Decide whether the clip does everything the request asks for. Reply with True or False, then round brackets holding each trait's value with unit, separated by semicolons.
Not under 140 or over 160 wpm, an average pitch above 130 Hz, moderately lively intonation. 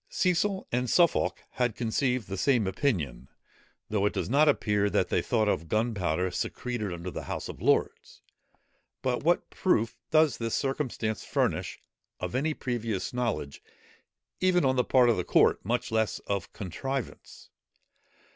False (150 wpm; 115 Hz; 4.8 semitones)